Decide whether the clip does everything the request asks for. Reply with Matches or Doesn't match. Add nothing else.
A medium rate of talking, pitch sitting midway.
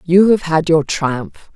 Matches